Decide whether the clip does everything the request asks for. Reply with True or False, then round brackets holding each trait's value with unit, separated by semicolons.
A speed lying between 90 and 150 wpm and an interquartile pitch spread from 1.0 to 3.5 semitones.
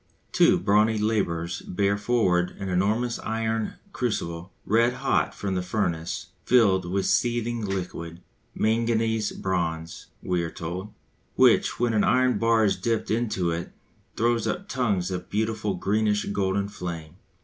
False (140 wpm; 3.9 semitones)